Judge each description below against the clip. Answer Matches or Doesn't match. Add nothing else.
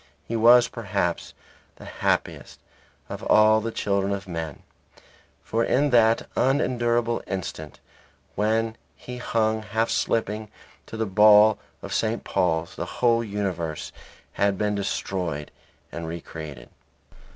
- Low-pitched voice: Matches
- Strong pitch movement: Doesn't match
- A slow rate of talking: Matches